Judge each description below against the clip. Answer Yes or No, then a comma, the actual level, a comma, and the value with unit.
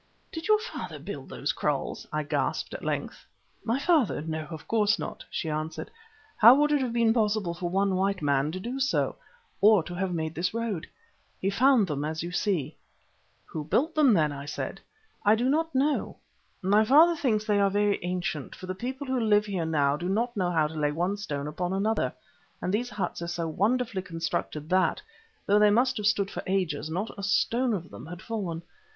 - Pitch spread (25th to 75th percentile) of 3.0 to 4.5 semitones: No, wide, 5.6 semitones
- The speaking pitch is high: Yes, high, 195 Hz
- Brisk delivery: Yes, fast, 210 wpm